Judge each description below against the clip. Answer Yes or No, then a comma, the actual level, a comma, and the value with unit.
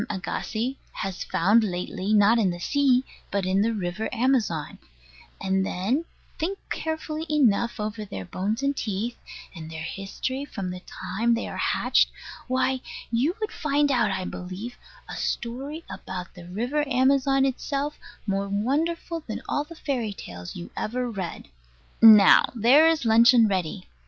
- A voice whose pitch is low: No, high, 230 Hz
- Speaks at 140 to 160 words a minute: Yes, average, 150 wpm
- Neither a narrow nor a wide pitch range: No, wide, 5.9 semitones